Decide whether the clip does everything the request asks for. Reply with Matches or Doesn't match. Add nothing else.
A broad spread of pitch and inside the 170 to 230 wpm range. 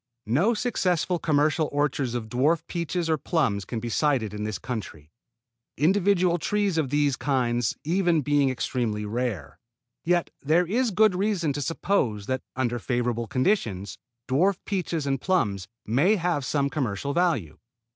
Doesn't match